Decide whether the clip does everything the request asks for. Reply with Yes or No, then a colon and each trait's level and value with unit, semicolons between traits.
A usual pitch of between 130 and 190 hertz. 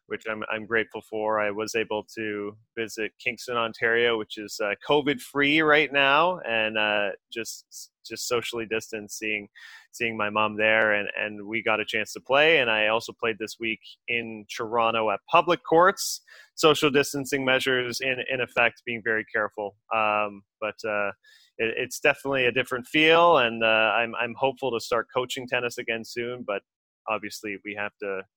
No: low, 115 Hz